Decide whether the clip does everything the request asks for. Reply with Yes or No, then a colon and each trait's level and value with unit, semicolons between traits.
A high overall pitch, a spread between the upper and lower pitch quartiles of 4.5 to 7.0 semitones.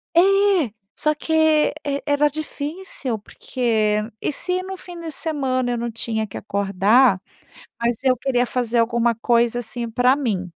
No: high, 245 Hz; average, 4.0 semitones